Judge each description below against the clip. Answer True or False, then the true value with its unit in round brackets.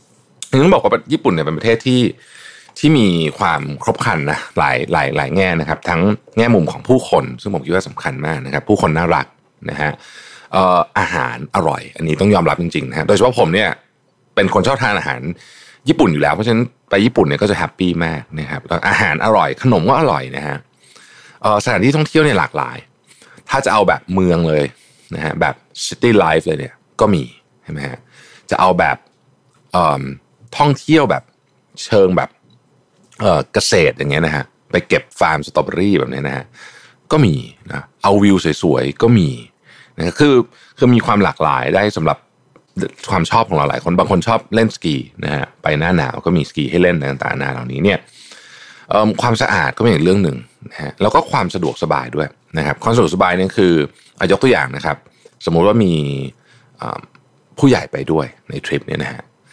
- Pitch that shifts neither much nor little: False (7.4 semitones)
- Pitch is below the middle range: True (90 Hz)